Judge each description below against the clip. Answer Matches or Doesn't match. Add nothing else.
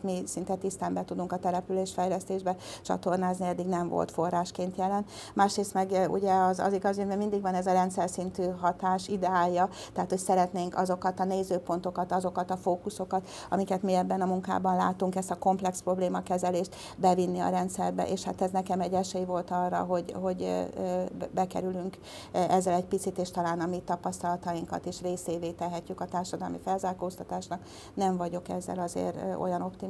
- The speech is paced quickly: Matches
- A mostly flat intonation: Matches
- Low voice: Doesn't match